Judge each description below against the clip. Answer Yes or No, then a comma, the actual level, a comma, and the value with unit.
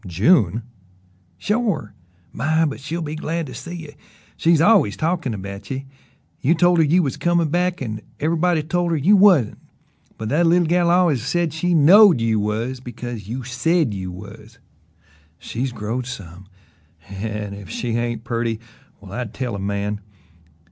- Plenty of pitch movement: Yes, wide, 7.7 semitones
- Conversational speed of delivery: Yes, average, 160 wpm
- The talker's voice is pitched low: Yes, low, 130 Hz